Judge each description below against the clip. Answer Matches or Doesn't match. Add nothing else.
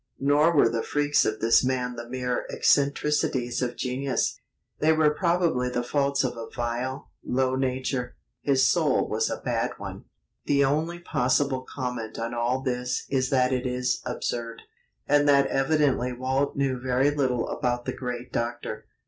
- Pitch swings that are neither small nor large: Doesn't match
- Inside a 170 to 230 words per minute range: Doesn't match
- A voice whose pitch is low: Matches